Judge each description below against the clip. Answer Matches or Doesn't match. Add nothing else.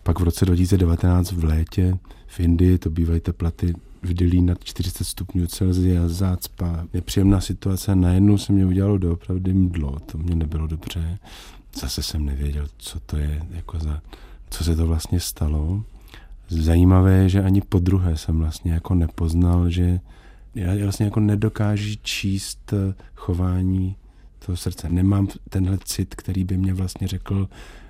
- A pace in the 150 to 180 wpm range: Matches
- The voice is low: Matches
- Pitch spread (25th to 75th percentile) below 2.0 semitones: Doesn't match